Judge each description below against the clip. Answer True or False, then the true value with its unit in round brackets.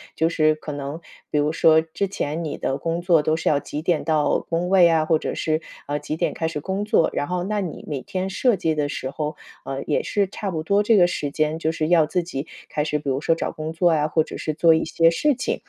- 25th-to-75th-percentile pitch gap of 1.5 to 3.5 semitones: True (2.6 semitones)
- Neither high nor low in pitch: True (160 Hz)